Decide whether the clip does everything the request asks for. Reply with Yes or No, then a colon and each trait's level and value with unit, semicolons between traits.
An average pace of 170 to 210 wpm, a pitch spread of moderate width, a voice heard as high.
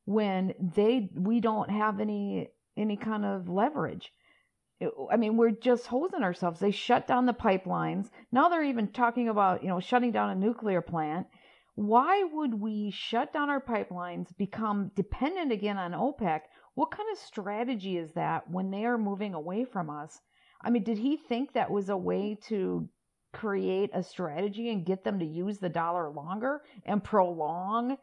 Yes: average, 175 wpm; average, 4.3 semitones; high, 210 Hz